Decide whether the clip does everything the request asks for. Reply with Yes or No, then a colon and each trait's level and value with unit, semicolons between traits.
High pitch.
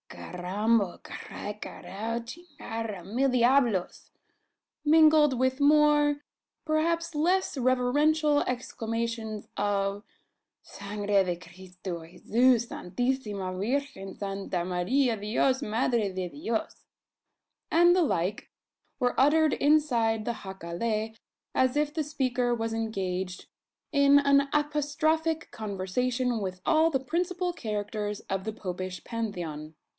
Yes: high, 235 Hz